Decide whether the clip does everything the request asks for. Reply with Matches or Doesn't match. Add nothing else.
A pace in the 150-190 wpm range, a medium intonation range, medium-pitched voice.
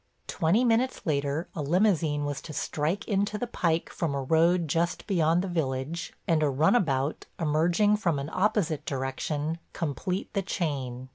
Matches